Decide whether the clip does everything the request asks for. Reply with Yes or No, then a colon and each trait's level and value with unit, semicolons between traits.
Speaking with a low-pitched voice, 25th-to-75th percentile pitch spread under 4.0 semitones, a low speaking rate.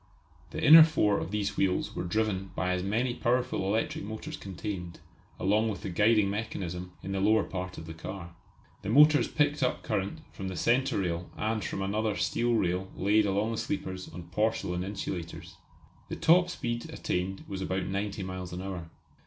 No: low, 100 Hz; average, 3.3 semitones; average, 180 wpm